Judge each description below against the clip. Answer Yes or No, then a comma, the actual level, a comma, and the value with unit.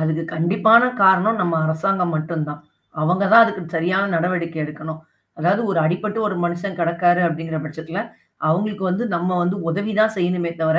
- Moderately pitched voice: Yes, medium, 175 Hz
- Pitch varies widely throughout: No, average, 3.2 semitones